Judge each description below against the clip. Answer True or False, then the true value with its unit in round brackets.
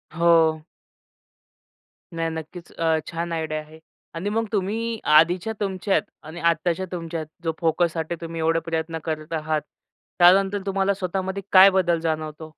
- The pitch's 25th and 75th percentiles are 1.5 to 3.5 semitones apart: True (2.8 semitones)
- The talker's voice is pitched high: False (165 Hz)